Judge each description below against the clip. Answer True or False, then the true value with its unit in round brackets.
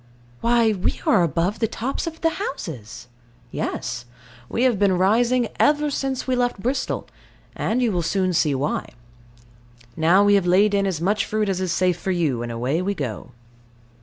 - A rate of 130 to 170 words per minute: False (180 wpm)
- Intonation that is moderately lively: False (5.8 semitones)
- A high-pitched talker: True (195 Hz)